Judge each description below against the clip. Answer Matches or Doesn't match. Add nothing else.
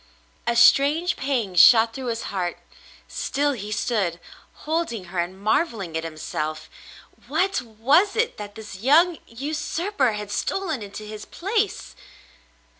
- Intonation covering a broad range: Matches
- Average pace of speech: Doesn't match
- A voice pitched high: Matches